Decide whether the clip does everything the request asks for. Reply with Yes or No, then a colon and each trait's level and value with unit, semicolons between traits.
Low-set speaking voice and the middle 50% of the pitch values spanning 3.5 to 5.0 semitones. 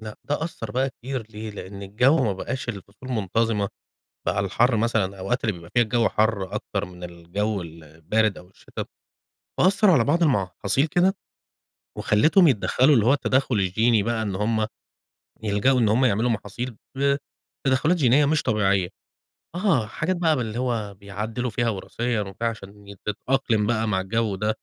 Yes: low, 110 Hz; average, 4.1 semitones